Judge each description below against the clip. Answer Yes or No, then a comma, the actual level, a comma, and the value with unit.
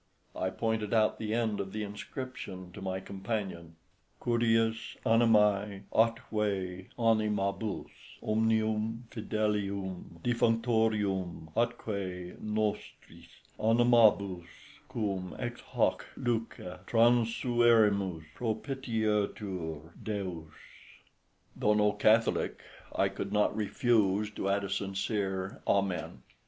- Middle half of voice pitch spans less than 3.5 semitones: Yes, average, 2.8 semitones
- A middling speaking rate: No, slow, 90 wpm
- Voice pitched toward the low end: Yes, low, 105 Hz